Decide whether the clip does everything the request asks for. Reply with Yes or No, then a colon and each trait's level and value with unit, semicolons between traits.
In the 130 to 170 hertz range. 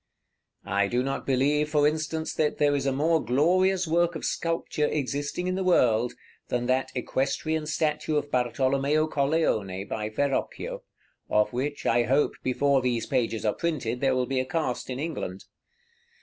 Yes: medium, 140 Hz